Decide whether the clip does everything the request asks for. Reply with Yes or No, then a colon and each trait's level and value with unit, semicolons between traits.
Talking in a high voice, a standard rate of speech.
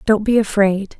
Yes: high, 205 Hz; average, 180 wpm